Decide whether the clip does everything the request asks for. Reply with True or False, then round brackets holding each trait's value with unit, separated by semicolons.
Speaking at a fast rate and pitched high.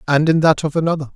False (260 wpm; 155 Hz)